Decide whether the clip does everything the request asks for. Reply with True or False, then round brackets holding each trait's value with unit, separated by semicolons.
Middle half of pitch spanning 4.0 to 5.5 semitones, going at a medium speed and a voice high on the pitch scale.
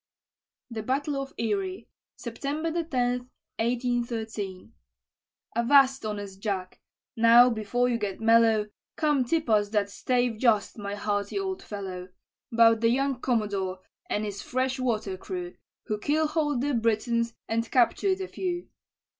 False (4.4 semitones; 130 wpm; 235 Hz)